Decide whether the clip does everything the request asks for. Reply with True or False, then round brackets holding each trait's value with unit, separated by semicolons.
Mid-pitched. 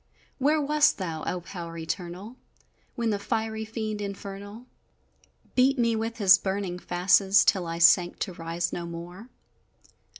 False (200 Hz)